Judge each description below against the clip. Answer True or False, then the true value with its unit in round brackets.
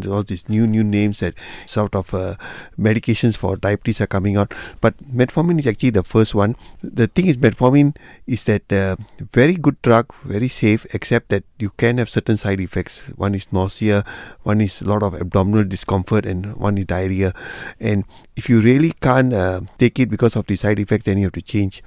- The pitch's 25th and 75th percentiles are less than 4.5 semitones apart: True (3.3 semitones)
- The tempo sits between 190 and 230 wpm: True (205 wpm)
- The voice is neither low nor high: False (105 Hz)